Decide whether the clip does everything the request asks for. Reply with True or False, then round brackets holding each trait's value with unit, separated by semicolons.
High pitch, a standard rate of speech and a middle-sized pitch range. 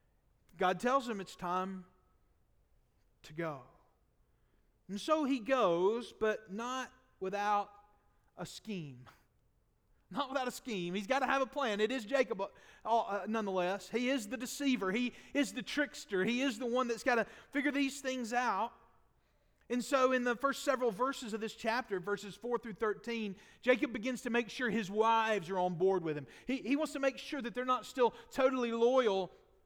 True (235 Hz; 180 wpm; 4.2 semitones)